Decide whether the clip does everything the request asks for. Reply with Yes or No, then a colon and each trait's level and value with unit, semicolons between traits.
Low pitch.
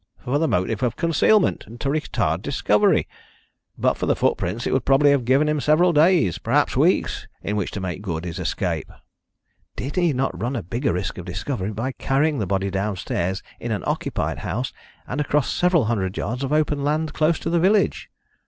Yes: low, 130 Hz